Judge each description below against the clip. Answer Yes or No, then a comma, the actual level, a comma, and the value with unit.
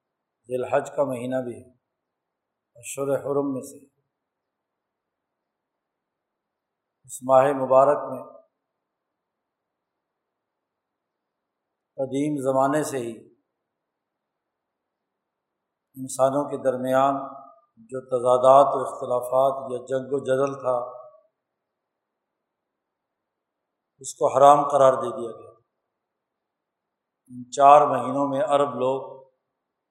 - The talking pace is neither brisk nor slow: No, slow, 85 wpm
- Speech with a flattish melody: Yes, narrow, 1.5 semitones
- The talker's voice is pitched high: No, low, 135 Hz